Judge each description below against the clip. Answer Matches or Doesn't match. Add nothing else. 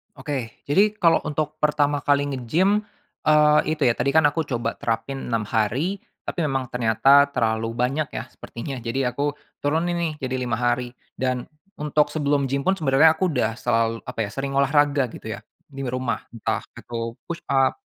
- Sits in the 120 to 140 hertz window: Matches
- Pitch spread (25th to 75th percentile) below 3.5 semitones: Doesn't match